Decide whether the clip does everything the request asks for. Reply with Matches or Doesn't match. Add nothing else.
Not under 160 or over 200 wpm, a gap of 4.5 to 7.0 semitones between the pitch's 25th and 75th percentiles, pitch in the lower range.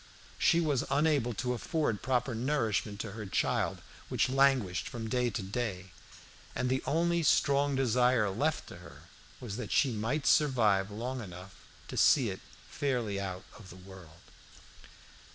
Doesn't match